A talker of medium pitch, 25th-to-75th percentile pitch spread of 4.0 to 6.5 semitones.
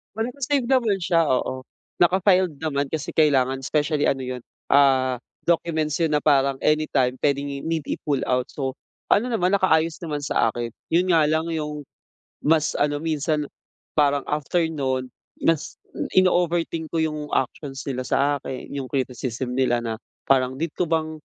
No: medium, 150 Hz; average, 3.5 semitones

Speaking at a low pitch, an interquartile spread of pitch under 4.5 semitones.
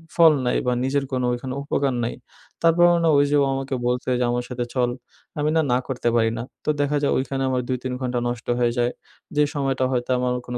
Yes: low, 130 Hz; narrow, 2.4 semitones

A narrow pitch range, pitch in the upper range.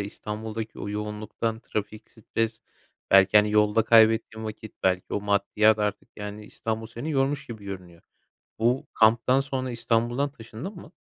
No: narrow, 1.9 semitones; low, 110 Hz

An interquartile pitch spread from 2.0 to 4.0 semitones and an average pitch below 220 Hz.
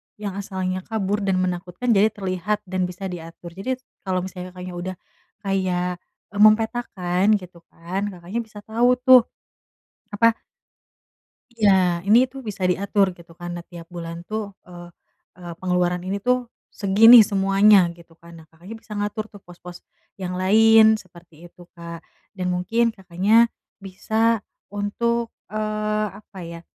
Yes: average, 3.0 semitones; high, 190 Hz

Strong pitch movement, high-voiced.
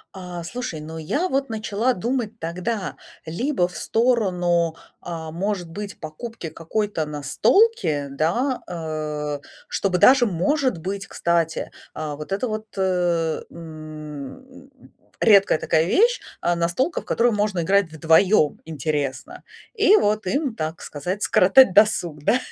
No: wide, 5.8 semitones; medium, 180 Hz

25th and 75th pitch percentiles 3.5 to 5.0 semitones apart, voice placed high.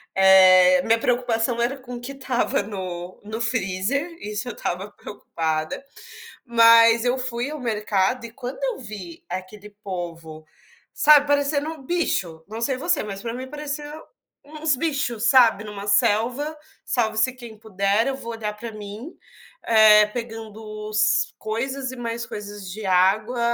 Yes: average, 3.9 semitones; high, 225 Hz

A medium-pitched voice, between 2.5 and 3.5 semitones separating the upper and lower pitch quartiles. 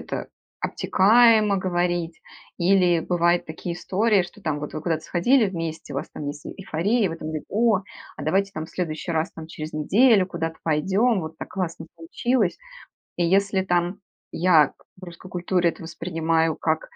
Yes: medium, 175 Hz; average, 3.2 semitones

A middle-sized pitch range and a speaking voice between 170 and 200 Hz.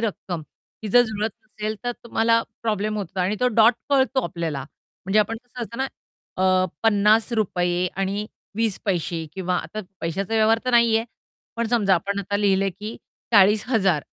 No: average, 3.1 semitones; high, 210 Hz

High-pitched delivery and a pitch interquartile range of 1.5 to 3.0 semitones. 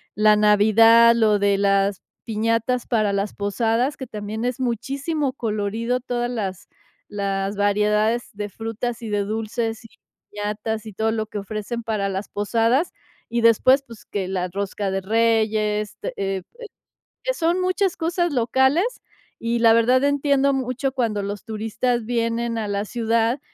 Yes: high, 225 Hz; average, 2.7 semitones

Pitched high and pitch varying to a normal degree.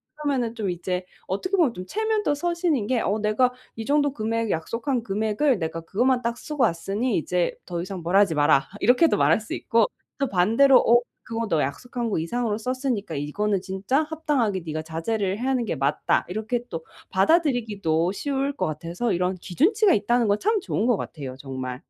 No: high, 220 Hz; wide, 6.3 semitones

